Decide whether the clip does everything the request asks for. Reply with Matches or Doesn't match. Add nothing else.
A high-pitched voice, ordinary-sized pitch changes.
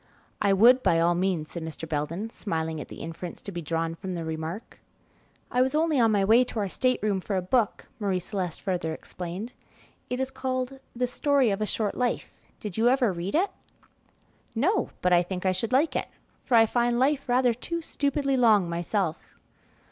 Doesn't match